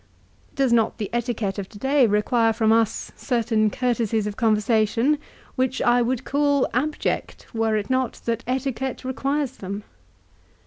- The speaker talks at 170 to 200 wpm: No, average, 145 wpm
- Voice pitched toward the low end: No, high, 235 Hz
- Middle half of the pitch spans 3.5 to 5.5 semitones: No, average, 3.1 semitones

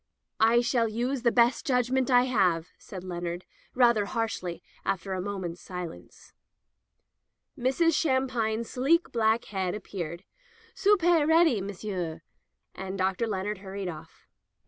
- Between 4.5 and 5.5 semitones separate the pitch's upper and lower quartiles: Yes, average, 5.1 semitones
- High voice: Yes, high, 220 Hz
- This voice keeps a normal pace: No, slow, 125 wpm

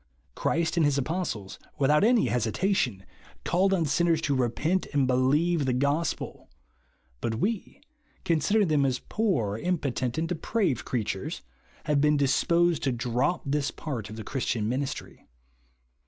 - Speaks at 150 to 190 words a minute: No, average, 140 wpm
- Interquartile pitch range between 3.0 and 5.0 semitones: No, wide, 5.4 semitones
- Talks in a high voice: No, medium, 145 Hz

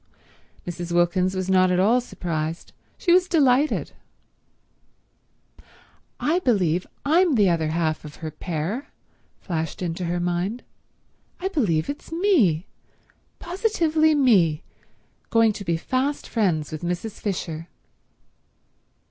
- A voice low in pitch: No, medium, 185 Hz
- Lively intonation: Yes, wide, 8.7 semitones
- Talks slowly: Yes, slow, 115 wpm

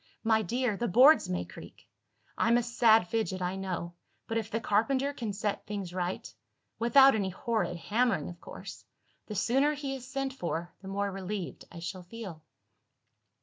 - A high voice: Yes, high, 215 Hz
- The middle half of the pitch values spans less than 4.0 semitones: No, average, 4.5 semitones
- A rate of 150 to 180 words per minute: Yes, average, 170 wpm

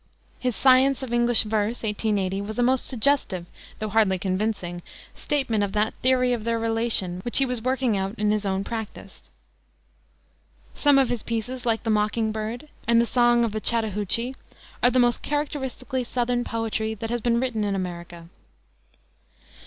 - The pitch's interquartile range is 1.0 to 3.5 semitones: Yes, average, 2.8 semitones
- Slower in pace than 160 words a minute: No, average, 165 wpm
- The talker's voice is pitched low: No, high, 230 Hz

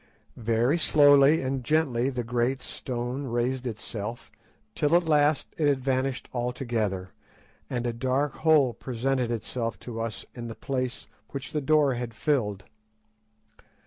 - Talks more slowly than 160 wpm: Yes, average, 140 wpm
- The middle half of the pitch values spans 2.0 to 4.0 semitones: Yes, average, 3.0 semitones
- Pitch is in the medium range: No, low, 130 Hz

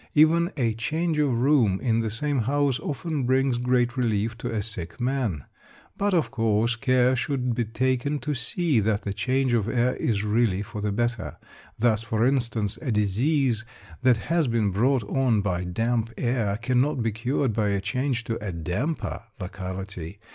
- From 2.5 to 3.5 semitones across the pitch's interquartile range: No, average, 3.9 semitones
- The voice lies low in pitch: Yes, low, 120 Hz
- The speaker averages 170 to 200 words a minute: Yes, average, 175 wpm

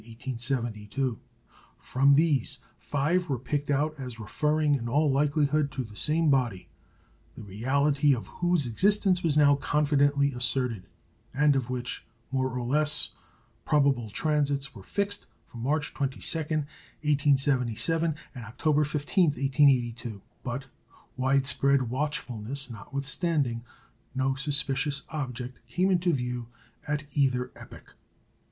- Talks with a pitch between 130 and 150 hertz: Yes, medium, 140 Hz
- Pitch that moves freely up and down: No, average, 3.0 semitones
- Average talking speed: No, slow, 115 wpm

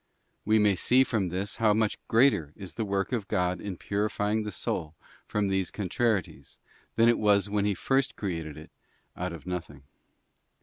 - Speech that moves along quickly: No, average, 175 wpm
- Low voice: Yes, low, 100 Hz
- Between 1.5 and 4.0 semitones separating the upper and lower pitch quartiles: Yes, average, 3.2 semitones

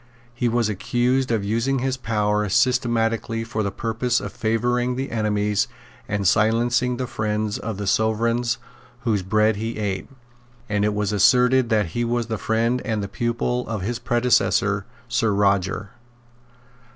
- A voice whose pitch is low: Yes, low, 115 Hz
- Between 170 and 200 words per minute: No, average, 150 wpm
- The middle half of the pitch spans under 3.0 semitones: Yes, narrow, 2.5 semitones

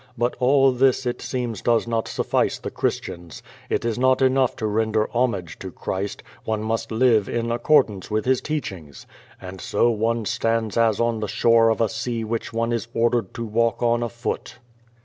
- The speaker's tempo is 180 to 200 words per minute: Yes, average, 185 wpm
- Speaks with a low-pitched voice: Yes, low, 115 Hz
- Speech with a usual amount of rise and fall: No, narrow, 1.8 semitones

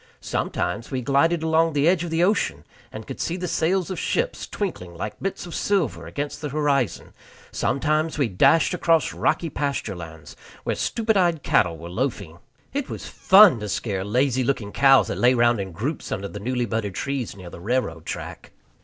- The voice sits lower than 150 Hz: Yes, medium, 140 Hz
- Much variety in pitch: Yes, wide, 8.0 semitones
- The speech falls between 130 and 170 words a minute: No, average, 190 wpm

